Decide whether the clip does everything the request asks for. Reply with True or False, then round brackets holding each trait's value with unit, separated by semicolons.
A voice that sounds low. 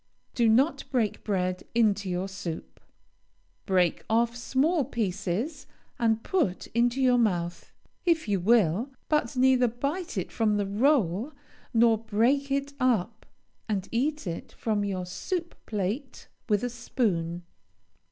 False (230 Hz)